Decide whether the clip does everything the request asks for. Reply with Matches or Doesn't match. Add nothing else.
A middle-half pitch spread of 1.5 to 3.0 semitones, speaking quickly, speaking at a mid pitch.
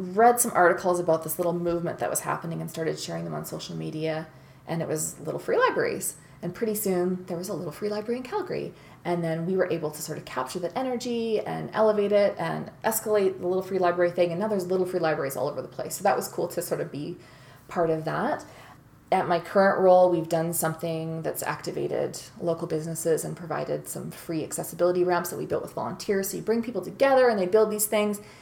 Doesn't match